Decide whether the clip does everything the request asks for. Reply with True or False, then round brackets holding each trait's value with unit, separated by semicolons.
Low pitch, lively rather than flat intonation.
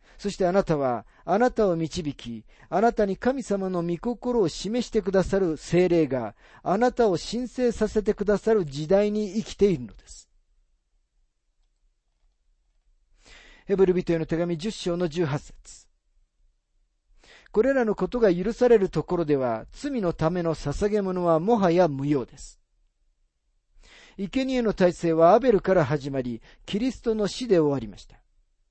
False (180 Hz; 6.2 semitones)